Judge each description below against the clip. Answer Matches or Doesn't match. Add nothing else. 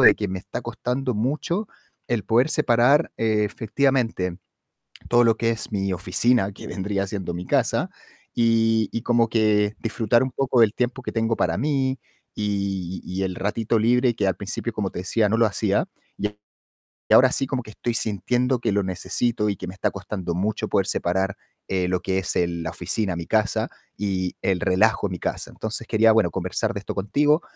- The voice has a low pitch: Matches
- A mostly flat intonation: Doesn't match